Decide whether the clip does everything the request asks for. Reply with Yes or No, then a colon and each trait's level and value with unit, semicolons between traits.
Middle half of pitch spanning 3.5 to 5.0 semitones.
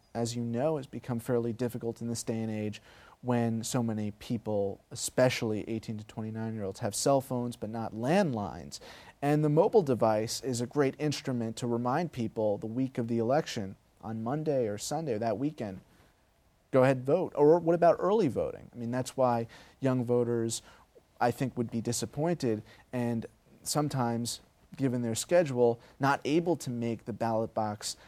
No: average, 2.8 semitones